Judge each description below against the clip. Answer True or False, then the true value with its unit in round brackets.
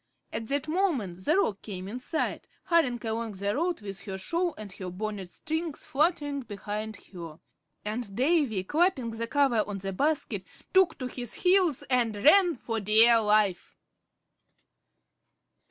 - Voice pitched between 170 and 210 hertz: False (230 Hz)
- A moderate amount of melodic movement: False (7.0 semitones)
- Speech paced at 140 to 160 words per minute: True (150 wpm)